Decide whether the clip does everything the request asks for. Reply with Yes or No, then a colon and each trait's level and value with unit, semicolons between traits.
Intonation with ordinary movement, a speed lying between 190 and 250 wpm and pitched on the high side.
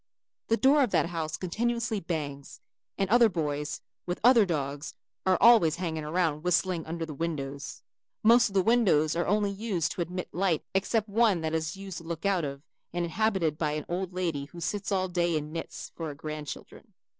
No: average, 4.1 semitones; average, 195 wpm; medium, 175 Hz